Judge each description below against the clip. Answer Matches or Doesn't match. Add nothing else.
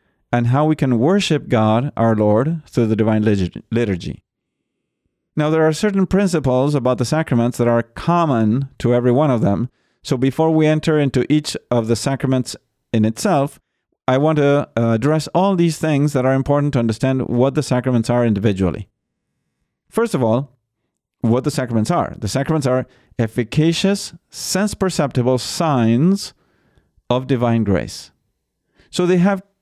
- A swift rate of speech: Doesn't match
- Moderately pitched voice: Doesn't match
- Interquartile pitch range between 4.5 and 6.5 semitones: Matches